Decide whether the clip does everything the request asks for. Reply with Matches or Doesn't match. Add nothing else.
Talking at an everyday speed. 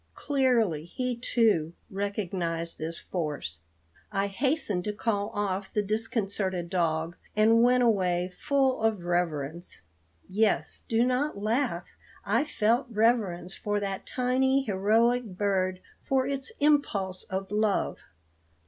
Doesn't match